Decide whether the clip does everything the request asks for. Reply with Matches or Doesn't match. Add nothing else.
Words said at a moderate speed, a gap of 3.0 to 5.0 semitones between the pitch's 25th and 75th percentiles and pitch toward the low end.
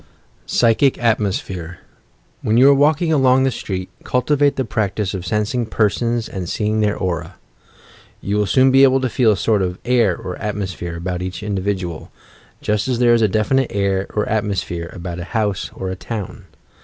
Matches